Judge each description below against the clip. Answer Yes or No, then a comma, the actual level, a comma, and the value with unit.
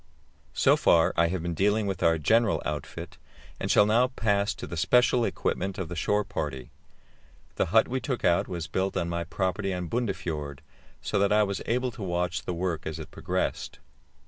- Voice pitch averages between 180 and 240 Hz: No, very low, 95 Hz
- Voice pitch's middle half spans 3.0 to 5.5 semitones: Yes, average, 4.0 semitones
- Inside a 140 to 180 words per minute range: No, average, 195 wpm